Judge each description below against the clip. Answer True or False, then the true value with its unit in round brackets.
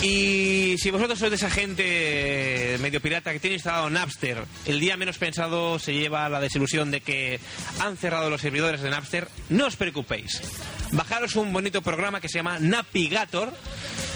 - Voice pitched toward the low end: False (170 Hz)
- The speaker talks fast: False (170 wpm)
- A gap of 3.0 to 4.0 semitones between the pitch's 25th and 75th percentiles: False (4.8 semitones)